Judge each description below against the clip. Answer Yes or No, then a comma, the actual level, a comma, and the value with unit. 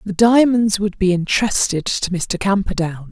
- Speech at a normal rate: Yes, average, 155 wpm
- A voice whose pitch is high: Yes, high, 195 Hz